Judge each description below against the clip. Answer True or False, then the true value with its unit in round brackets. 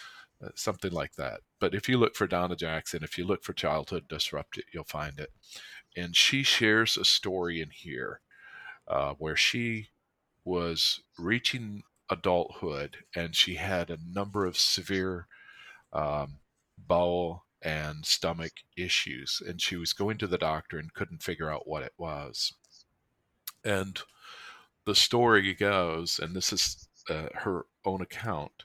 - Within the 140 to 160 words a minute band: True (145 wpm)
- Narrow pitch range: False (3.7 semitones)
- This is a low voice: True (90 Hz)